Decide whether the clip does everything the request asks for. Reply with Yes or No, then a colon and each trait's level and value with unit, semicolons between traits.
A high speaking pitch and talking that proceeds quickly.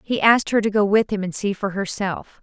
Yes: high, 205 Hz; fast, 275 wpm